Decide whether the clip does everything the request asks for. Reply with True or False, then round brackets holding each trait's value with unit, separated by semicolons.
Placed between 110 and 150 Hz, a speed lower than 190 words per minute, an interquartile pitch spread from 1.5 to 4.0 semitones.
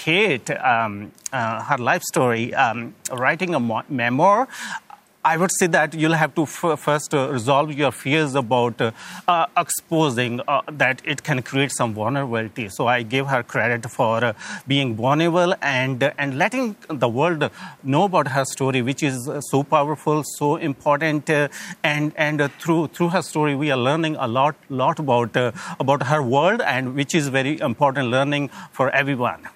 True (140 Hz; 180 wpm; 3.5 semitones)